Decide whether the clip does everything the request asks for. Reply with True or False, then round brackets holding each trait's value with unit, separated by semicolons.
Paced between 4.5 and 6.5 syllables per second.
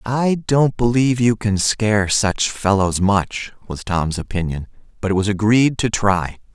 False (4.3 syllables/s)